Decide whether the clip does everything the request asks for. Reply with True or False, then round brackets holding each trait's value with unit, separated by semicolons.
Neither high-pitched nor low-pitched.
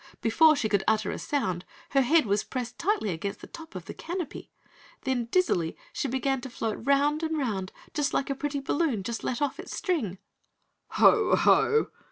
False (265 Hz)